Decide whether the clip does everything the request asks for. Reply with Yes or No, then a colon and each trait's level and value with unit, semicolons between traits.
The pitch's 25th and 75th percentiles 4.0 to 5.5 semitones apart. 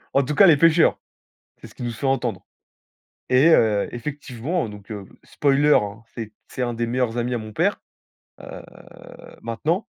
Yes: average, 4.5 semitones